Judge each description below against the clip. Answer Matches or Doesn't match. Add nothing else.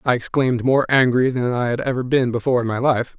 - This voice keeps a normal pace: Doesn't match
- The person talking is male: Matches